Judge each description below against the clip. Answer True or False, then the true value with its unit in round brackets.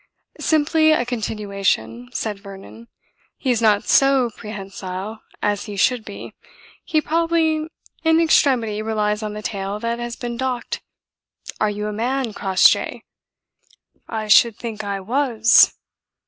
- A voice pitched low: False (220 Hz)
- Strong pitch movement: False (3.7 semitones)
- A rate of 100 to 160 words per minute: True (135 wpm)